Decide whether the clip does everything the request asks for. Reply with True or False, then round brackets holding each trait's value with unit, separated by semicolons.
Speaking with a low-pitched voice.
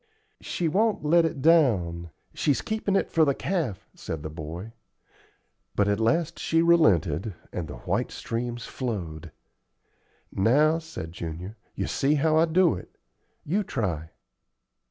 True (125 Hz)